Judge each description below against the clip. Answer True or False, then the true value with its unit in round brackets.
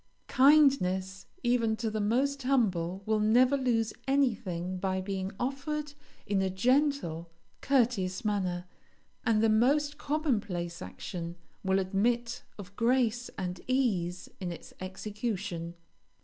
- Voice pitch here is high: True (215 Hz)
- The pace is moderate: False (120 wpm)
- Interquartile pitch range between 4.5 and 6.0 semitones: True (5.2 semitones)